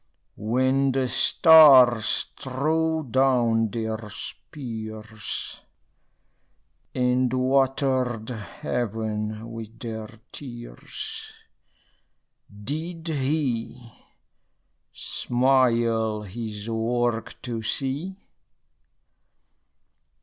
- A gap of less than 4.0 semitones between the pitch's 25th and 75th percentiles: Yes, average, 3.1 semitones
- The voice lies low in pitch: Yes, low, 120 Hz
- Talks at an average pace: No, slow, 60 wpm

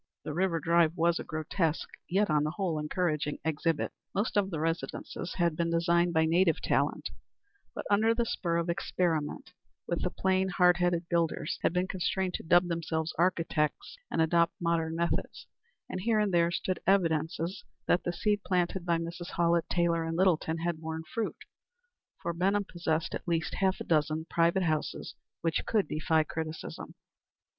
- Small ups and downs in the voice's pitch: Yes, narrow, 2.0 semitones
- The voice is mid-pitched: Yes, medium, 170 Hz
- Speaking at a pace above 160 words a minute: Yes, average, 170 wpm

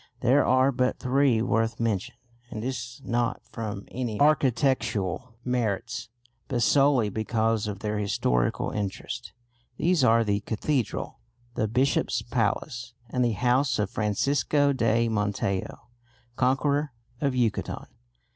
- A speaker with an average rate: No, slow, 120 wpm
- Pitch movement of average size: Yes, average, 3.1 semitones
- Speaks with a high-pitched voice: No, low, 120 Hz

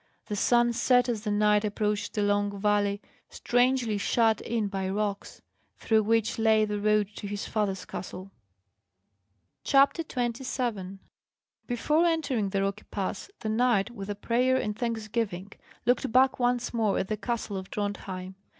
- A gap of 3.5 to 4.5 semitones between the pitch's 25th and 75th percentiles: No, average, 2.9 semitones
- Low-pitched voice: No, high, 215 Hz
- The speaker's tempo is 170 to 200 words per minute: No, average, 150 wpm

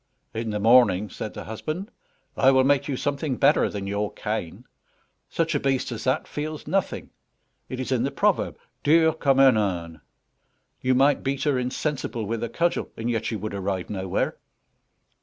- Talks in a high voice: No, low, 125 Hz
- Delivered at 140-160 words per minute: No, average, 175 wpm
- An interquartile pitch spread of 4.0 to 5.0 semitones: Yes, average, 4.7 semitones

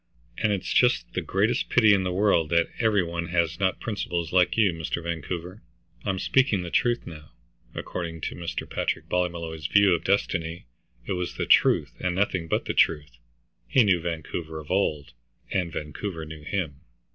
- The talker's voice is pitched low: Yes, very low, 85 Hz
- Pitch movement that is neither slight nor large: Yes, average, 3.2 semitones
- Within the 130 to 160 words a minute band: No, average, 175 wpm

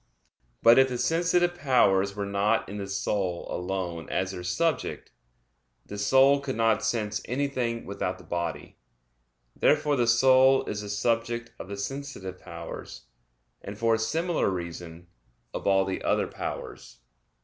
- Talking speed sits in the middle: Yes, average, 150 wpm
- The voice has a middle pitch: No, low, 110 Hz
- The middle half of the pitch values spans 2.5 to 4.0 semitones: No, wide, 5.5 semitones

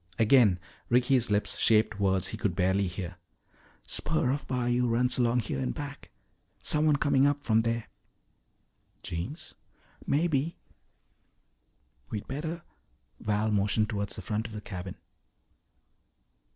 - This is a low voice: Yes, low, 115 Hz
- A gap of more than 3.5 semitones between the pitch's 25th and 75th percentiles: Yes, average, 4.8 semitones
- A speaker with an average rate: No, slow, 125 wpm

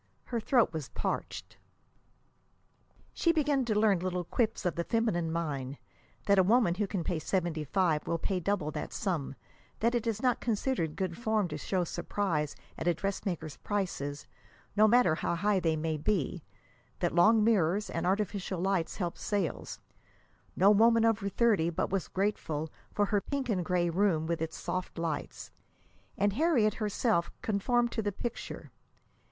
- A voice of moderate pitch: No, high, 195 Hz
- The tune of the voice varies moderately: Yes, average, 4.4 semitones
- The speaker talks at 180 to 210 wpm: No, average, 165 wpm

